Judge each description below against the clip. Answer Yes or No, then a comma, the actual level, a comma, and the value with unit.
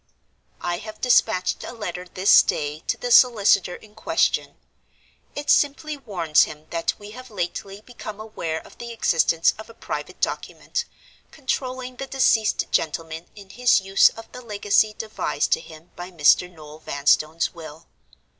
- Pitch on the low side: No, high, 200 Hz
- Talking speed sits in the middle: Yes, average, 155 wpm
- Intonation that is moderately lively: No, wide, 6.0 semitones